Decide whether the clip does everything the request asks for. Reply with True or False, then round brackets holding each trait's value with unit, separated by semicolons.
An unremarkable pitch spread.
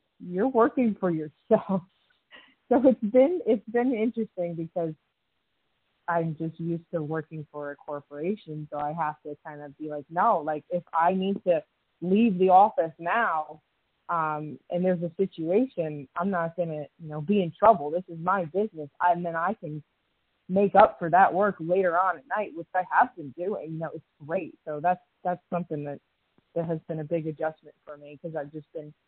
True (3.8 semitones)